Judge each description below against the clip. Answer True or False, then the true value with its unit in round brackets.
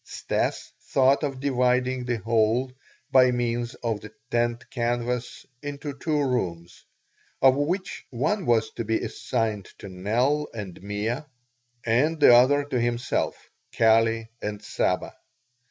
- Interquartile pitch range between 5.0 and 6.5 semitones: False (3.0 semitones)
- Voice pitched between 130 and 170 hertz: False (120 Hz)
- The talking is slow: True (130 wpm)